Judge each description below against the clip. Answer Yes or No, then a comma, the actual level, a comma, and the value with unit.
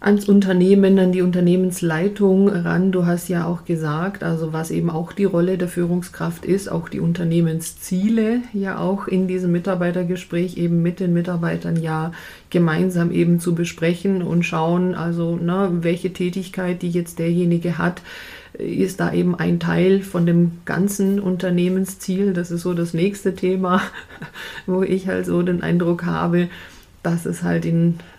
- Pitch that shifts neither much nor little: No, narrow, 1.5 semitones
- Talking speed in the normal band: Yes, average, 155 wpm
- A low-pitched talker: No, medium, 175 Hz